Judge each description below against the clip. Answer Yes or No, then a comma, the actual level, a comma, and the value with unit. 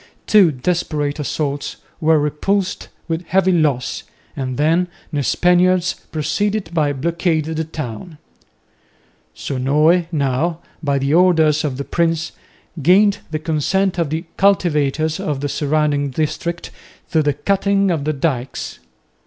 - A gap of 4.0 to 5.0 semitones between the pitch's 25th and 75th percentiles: No, average, 3.4 semitones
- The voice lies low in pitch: No, medium, 155 Hz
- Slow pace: Yes, slow, 130 wpm